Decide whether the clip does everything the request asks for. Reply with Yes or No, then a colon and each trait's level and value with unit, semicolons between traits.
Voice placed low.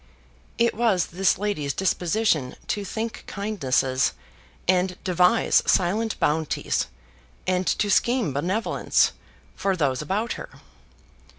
No: medium, 185 Hz